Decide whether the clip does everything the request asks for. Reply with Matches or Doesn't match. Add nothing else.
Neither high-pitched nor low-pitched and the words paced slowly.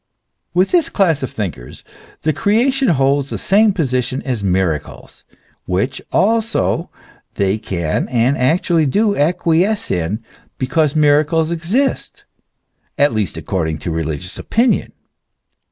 Matches